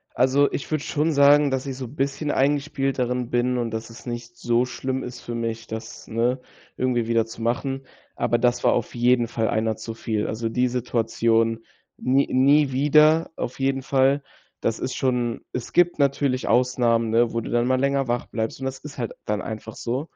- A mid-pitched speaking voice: No, low, 125 Hz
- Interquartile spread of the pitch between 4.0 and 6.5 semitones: No, average, 2.7 semitones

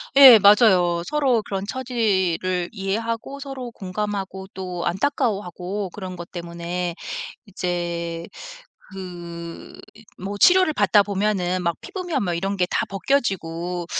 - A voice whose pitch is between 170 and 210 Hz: Yes, high, 190 Hz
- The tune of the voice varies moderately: Yes, average, 3.9 semitones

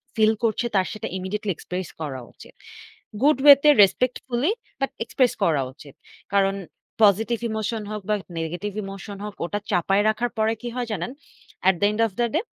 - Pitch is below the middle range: No, high, 210 Hz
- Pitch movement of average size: Yes, average, 3.6 semitones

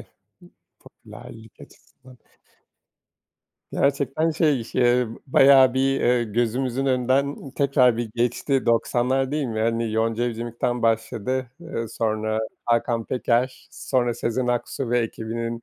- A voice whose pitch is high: No, low, 120 Hz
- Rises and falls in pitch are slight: Yes, narrow, 2.3 semitones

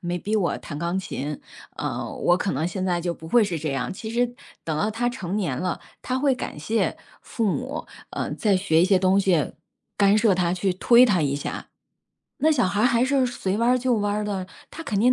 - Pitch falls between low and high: No, high, 195 Hz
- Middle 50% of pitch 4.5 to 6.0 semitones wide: Yes, average, 5.2 semitones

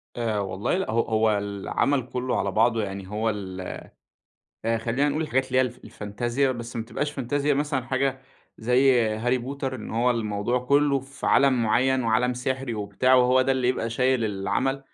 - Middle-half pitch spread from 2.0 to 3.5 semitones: Yes, average, 3.1 semitones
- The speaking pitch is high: No, low, 125 Hz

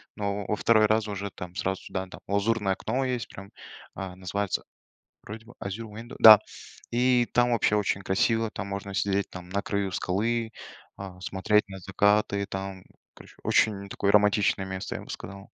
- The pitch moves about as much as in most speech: No, narrow, 2.3 semitones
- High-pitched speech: No, low, 100 Hz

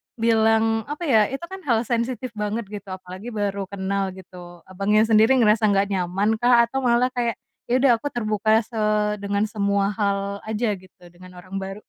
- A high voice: Yes, high, 210 Hz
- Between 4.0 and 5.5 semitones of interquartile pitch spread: No, average, 2.9 semitones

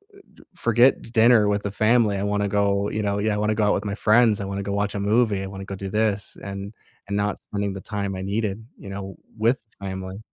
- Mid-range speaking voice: No, low, 100 Hz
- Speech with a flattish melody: Yes, narrow, 1.7 semitones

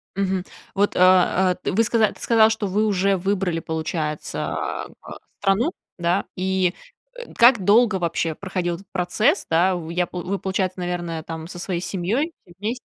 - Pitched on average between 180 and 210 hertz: Yes, high, 190 Hz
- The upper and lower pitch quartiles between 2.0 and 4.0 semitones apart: Yes, average, 2.8 semitones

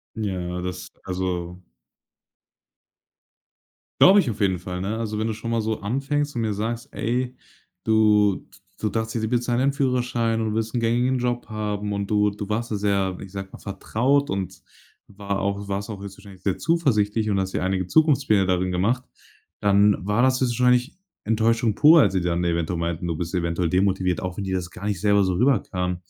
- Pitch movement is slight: No, average, 3.8 semitones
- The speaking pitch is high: No, low, 105 Hz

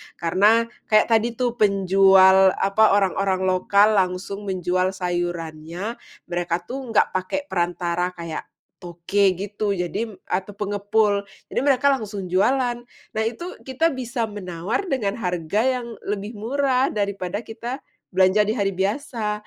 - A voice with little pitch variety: No, average, 3.7 semitones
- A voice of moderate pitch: No, high, 200 Hz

